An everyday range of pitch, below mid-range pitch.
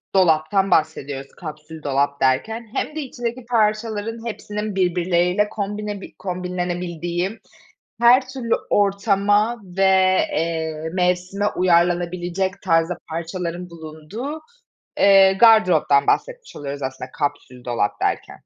No: average, 4.4 semitones; medium, 180 Hz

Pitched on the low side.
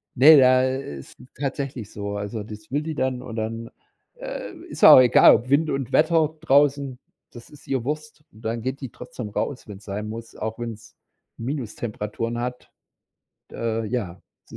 Yes: low, 120 Hz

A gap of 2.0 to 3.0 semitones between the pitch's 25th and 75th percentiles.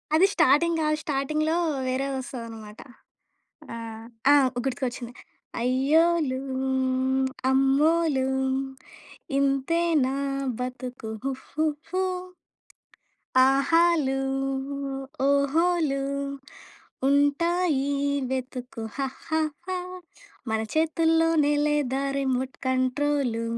No: average, 3.5 semitones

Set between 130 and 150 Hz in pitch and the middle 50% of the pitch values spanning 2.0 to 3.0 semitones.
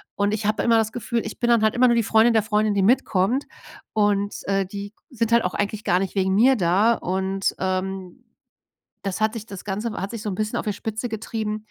No: high, 210 Hz; narrow, 2.5 semitones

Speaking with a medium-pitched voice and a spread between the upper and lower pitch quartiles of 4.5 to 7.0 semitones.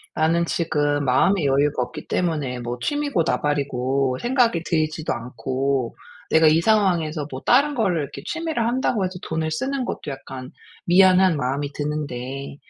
Yes: medium, 155 Hz; average, 5.3 semitones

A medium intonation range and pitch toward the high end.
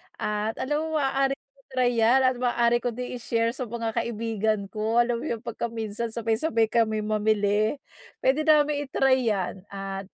Yes: average, 3.2 semitones; high, 230 Hz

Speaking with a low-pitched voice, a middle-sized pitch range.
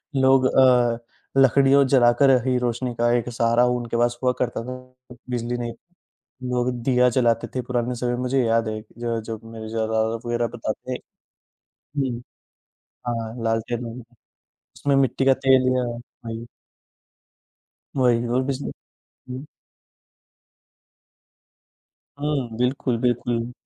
No: low, 120 Hz; narrow, 1.6 semitones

